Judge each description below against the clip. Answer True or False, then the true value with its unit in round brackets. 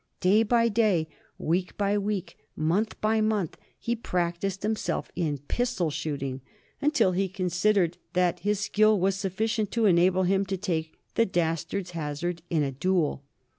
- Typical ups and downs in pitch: True (3.7 semitones)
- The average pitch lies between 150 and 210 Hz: True (185 Hz)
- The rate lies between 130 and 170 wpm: True (150 wpm)